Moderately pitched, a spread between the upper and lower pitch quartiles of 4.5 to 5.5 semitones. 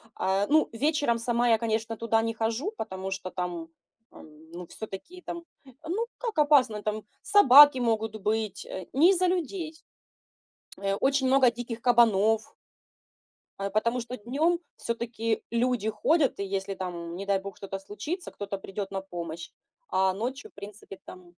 No: high, 225 Hz; average, 5.1 semitones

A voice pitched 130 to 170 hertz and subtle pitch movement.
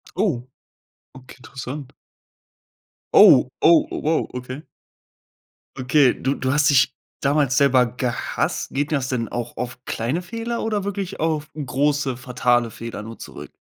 No: low, 135 Hz; average, 3.3 semitones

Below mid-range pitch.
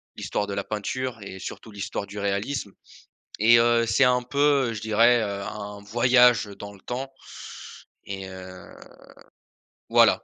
Yes: low, 110 Hz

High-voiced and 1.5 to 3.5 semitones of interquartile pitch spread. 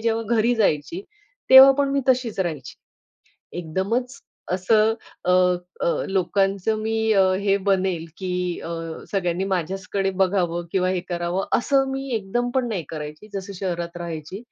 No: high, 195 Hz; average, 4.0 semitones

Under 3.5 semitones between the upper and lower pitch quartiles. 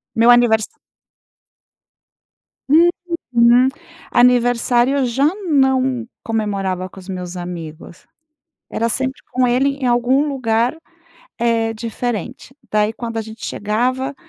Yes: average, 2.9 semitones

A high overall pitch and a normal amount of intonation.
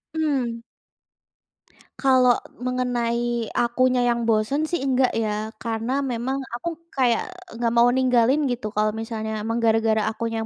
No: high, 240 Hz; narrow, 2.3 semitones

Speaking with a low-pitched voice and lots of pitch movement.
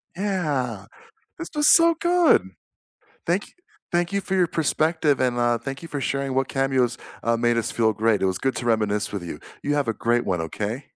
Yes: low, 130 Hz; wide, 6.1 semitones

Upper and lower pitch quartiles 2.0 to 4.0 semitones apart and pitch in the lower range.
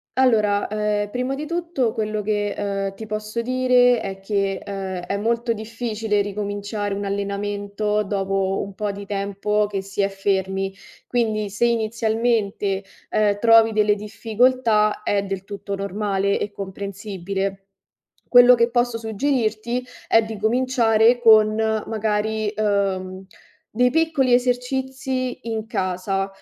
No: narrow, 2.6 semitones; high, 210 Hz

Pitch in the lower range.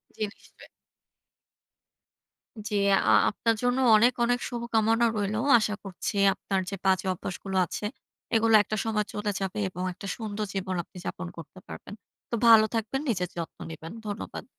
No: high, 210 Hz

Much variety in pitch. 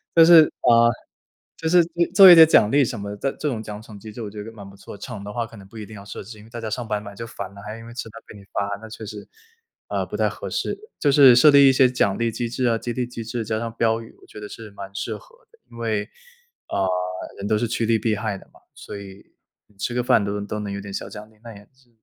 No: average, 2.8 semitones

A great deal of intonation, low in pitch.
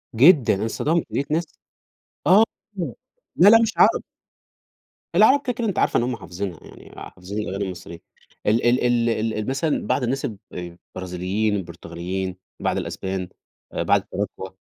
Yes: wide, 7.9 semitones; low, 105 Hz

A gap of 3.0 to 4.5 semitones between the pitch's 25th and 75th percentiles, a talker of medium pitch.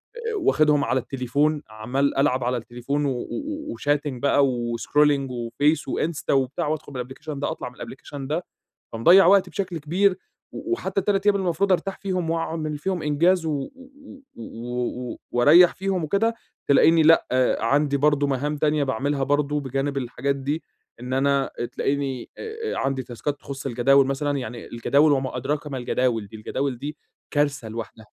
Yes: average, 3.7 semitones; medium, 145 Hz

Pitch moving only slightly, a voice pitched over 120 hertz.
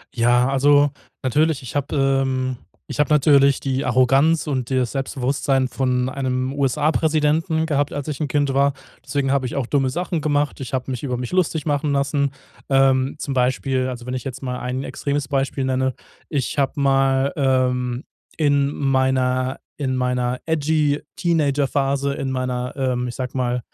Yes: narrow, 1.9 semitones; low, 135 Hz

